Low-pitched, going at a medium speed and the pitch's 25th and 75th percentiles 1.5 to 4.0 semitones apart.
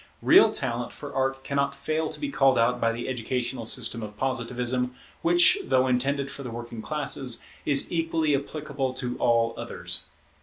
Yes: low, 130 Hz; average, 165 wpm; average, 2.8 semitones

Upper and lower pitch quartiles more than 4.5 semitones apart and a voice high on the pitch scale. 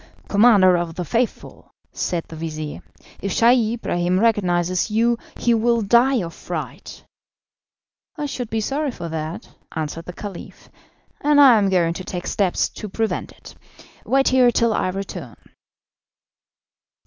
Yes: average, 5.3 semitones; high, 205 Hz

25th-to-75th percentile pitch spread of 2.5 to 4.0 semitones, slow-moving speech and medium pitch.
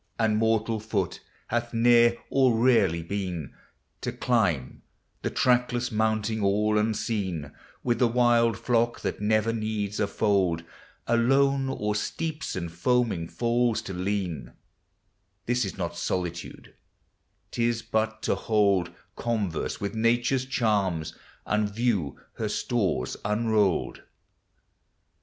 No: average, 3.4 semitones; slow, 120 wpm; low, 110 Hz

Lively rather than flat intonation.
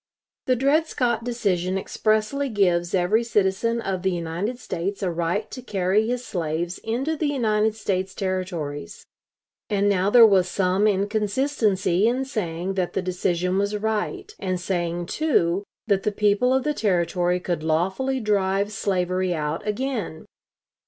No: average, 3.9 semitones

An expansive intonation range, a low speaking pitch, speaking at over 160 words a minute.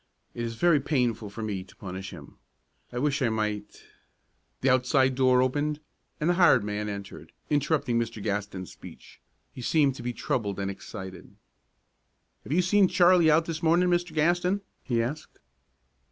Yes: wide, 6.9 semitones; low, 130 Hz; average, 170 wpm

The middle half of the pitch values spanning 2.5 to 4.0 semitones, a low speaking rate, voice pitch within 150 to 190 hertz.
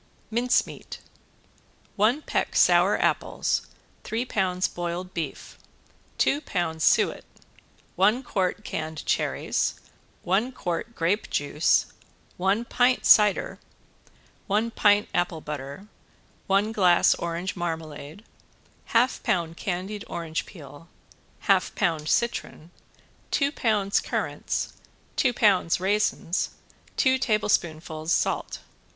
No: average, 4.4 semitones; slow, 100 wpm; medium, 185 Hz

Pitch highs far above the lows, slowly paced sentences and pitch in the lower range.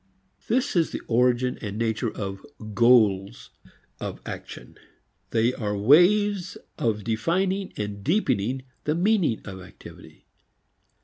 Yes: wide, 8.8 semitones; slow, 115 wpm; low, 120 Hz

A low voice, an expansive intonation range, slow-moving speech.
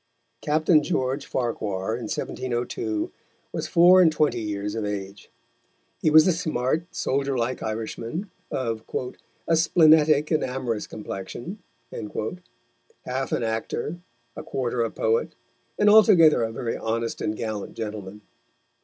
Yes: low, 125 Hz; wide, 5.9 semitones; slow, 125 wpm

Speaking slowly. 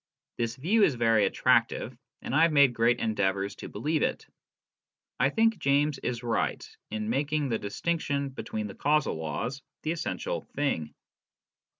No: average, 155 wpm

